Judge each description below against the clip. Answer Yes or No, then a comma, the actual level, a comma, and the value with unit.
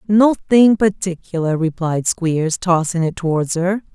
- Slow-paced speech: Yes, slow, 120 wpm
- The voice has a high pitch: No, medium, 180 Hz